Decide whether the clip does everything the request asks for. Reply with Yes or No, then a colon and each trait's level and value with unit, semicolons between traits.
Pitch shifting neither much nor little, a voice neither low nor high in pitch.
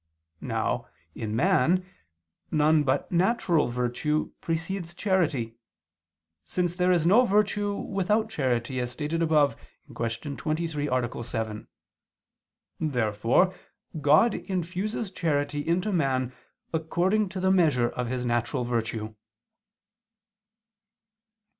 No: wide, 6.7 semitones; medium, 155 Hz